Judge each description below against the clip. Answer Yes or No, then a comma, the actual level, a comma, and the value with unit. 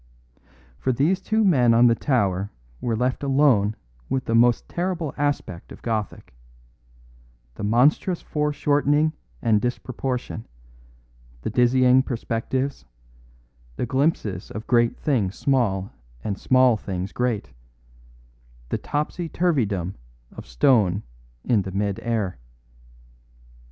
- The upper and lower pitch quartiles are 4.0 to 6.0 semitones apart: Yes, average, 5.2 semitones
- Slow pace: Yes, slow, 110 wpm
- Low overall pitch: Yes, low, 120 Hz